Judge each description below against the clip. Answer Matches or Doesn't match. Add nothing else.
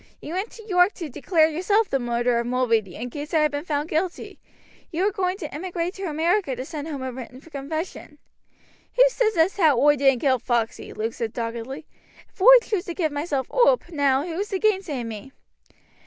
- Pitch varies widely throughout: Matches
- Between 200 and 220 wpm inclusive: Matches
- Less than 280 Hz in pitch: Doesn't match